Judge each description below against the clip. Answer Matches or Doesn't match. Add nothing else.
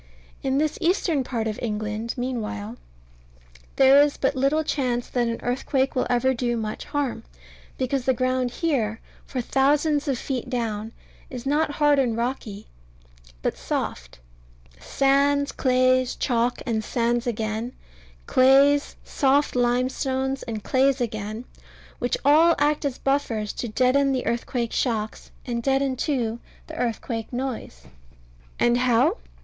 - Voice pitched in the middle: Doesn't match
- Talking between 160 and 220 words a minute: Doesn't match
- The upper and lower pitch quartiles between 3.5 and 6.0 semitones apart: Doesn't match